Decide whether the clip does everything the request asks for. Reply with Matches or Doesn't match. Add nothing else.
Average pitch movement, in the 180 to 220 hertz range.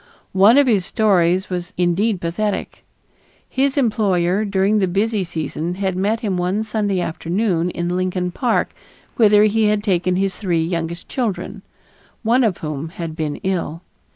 Matches